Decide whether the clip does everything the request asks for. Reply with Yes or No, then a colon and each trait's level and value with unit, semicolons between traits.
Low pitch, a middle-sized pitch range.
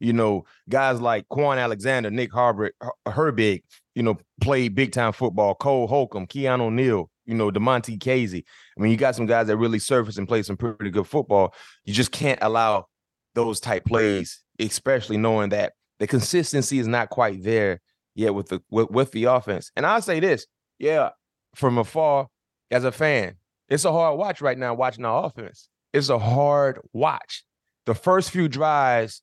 Yes: low, 120 Hz; average, 3.6 semitones